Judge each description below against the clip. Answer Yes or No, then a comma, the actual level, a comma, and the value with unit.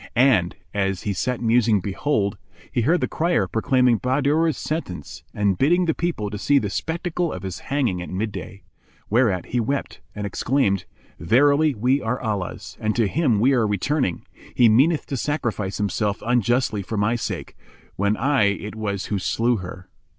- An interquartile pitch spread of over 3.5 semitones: Yes, wide, 5.4 semitones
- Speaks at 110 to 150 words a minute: No, average, 170 wpm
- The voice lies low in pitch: Yes, low, 115 Hz